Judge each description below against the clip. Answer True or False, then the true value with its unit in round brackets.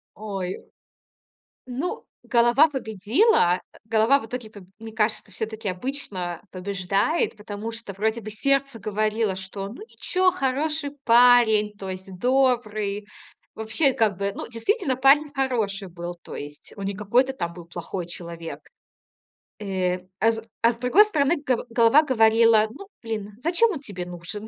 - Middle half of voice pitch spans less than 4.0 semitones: False (4.7 semitones)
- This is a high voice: True (220 Hz)